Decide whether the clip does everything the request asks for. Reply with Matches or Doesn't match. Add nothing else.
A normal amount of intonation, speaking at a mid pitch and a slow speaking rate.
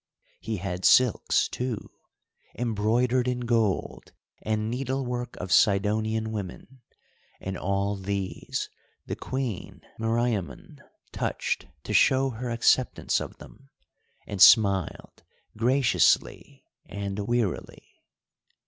Doesn't match